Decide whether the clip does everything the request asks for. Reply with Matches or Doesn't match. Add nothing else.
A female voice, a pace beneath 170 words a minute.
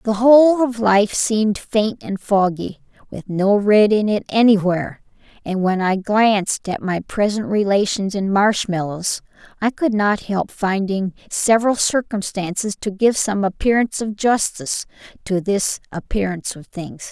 Matches